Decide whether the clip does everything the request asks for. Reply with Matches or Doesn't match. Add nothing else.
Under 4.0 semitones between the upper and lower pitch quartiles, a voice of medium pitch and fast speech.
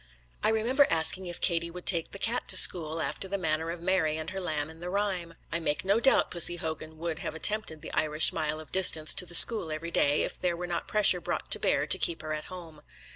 Matches